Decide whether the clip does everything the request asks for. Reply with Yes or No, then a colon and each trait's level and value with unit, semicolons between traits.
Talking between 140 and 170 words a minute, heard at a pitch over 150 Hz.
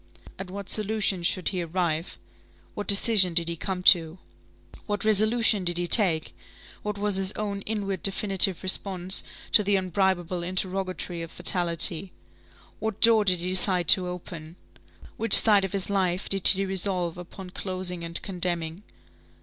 Yes: average, 150 wpm; medium, 185 Hz